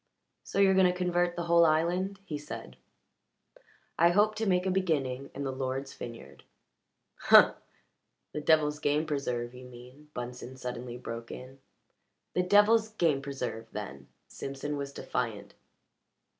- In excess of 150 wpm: No, average, 145 wpm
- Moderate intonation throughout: No, wide, 5.8 semitones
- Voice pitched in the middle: Yes, medium, 145 Hz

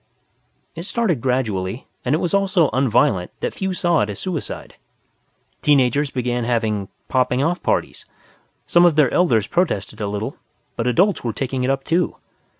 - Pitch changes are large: Yes, wide, 6.8 semitones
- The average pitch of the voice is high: No, low, 130 Hz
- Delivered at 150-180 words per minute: Yes, average, 175 wpm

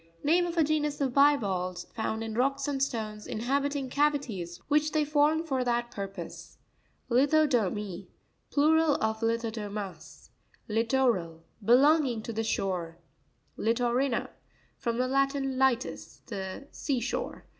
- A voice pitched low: No, high, 245 Hz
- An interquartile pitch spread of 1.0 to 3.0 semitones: No, average, 4.8 semitones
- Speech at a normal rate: No, slow, 115 wpm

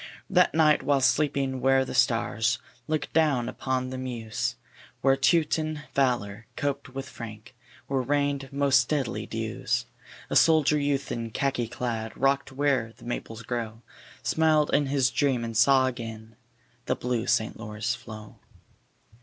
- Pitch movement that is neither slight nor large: Yes, average, 3.4 semitones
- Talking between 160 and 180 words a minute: No, average, 145 wpm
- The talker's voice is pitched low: Yes, low, 130 Hz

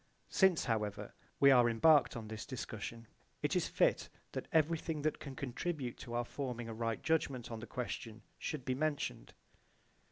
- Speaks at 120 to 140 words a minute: No, average, 165 wpm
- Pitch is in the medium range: No, low, 125 Hz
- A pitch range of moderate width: Yes, average, 4.6 semitones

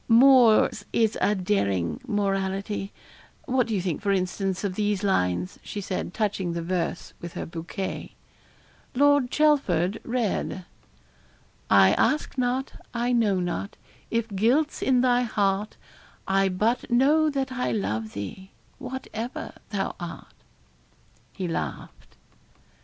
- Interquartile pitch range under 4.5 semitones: No, average, 5.1 semitones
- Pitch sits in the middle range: No, high, 205 Hz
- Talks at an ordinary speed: No, slow, 125 wpm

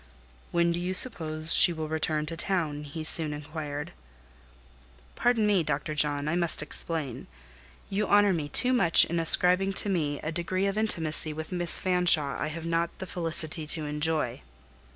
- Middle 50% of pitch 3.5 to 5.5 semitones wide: No, average, 2.8 semitones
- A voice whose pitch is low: No, medium, 165 Hz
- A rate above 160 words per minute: Yes, average, 170 wpm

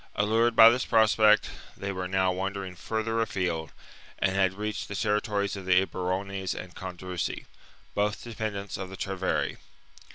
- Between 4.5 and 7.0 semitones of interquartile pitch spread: No, narrow, 2.4 semitones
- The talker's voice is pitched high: No, low, 100 Hz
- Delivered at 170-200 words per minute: No, average, 155 wpm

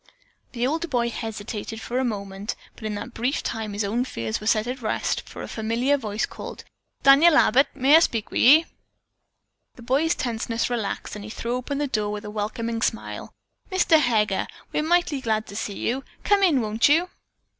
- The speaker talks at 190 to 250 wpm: Yes, average, 195 wpm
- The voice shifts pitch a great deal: No, average, 4.2 semitones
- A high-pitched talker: Yes, high, 235 Hz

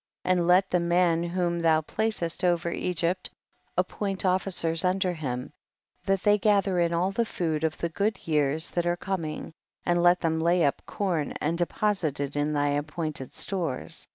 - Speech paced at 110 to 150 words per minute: No, average, 180 wpm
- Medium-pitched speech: Yes, medium, 170 Hz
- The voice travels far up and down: No, average, 2.7 semitones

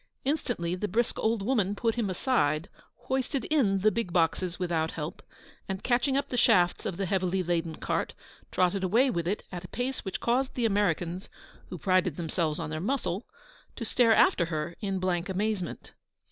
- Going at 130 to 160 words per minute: No, average, 180 wpm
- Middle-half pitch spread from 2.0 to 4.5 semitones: No, average, 5.0 semitones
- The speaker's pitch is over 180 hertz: Yes, high, 190 Hz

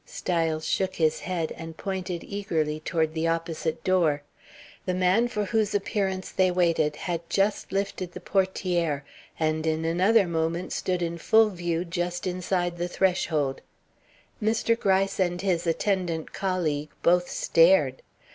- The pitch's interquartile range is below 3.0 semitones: Yes, narrow, 2.6 semitones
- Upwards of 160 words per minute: No, average, 140 wpm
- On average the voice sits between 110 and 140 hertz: No, medium, 175 Hz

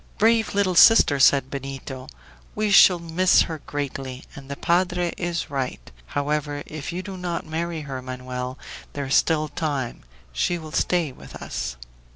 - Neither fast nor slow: Yes, average, 160 wpm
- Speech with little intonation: No, average, 4.5 semitones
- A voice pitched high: No, medium, 150 Hz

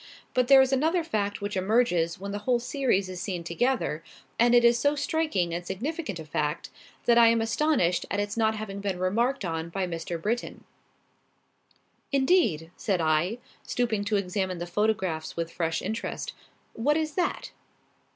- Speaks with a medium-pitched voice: No, high, 205 Hz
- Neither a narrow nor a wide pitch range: No, wide, 5.7 semitones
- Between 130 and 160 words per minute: No, average, 170 wpm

